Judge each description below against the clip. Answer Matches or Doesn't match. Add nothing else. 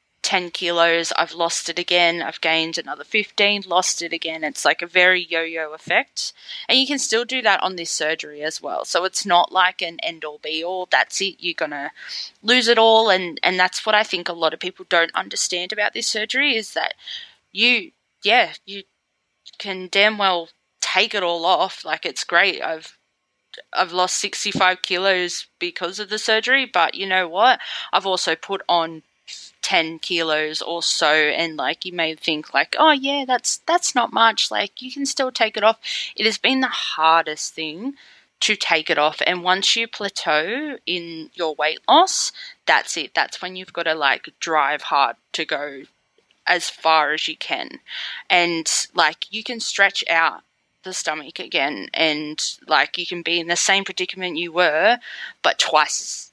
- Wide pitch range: Doesn't match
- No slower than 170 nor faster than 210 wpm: Matches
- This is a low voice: Doesn't match